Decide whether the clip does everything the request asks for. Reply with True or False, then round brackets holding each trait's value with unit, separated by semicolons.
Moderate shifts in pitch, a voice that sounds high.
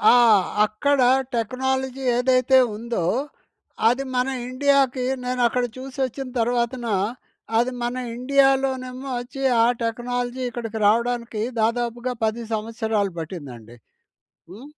False (2.2 semitones; 245 Hz)